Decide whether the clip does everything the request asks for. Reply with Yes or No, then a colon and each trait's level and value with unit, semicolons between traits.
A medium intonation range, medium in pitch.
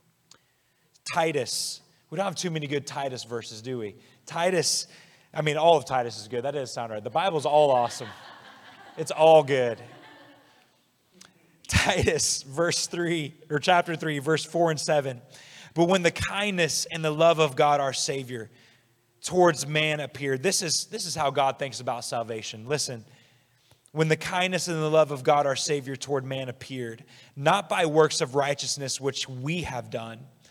Yes: average, 4.3 semitones; medium, 145 Hz